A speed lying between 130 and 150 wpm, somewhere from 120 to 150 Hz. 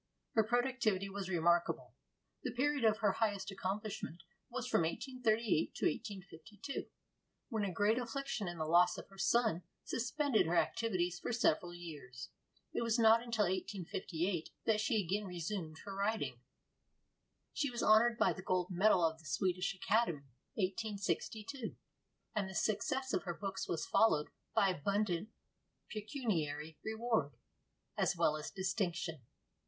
No: average, 140 wpm; high, 200 Hz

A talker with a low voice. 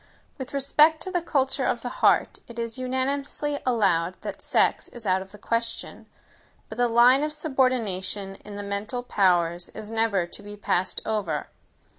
No: high, 230 Hz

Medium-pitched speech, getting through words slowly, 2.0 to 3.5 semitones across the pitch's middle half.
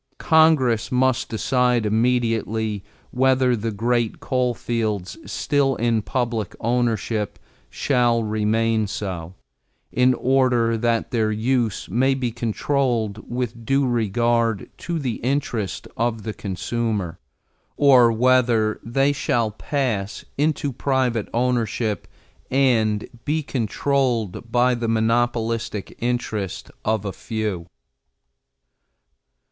No: low, 115 Hz; slow, 105 wpm; narrow, 2.6 semitones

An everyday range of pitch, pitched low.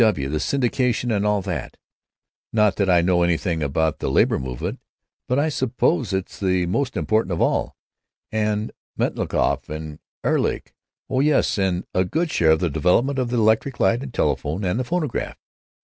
No: wide, 6.2 semitones; low, 105 Hz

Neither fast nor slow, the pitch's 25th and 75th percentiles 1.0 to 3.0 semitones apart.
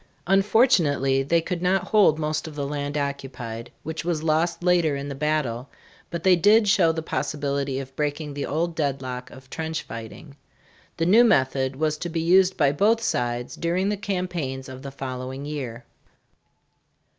No: average, 170 wpm; average, 4.3 semitones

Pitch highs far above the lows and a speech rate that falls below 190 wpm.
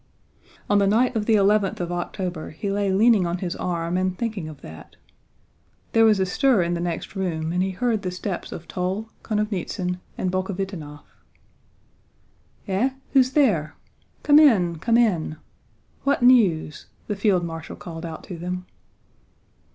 No: average, 3.7 semitones; average, 160 wpm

